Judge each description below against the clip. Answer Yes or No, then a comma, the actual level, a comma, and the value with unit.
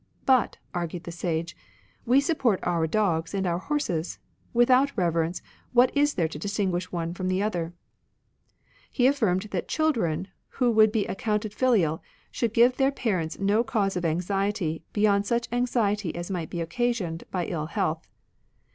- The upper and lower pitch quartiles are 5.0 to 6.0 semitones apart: Yes, wide, 5.6 semitones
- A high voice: Yes, high, 195 Hz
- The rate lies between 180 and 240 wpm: No, average, 170 wpm